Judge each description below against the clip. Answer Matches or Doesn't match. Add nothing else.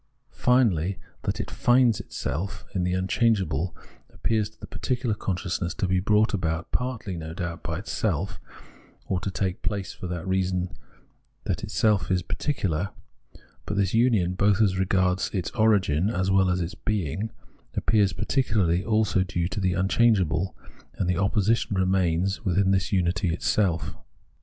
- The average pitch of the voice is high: Doesn't match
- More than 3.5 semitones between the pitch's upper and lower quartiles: Doesn't match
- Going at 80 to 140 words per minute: Doesn't match